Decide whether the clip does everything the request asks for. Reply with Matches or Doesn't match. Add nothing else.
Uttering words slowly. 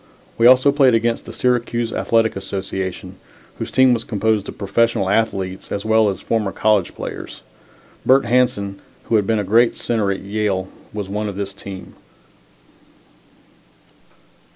Doesn't match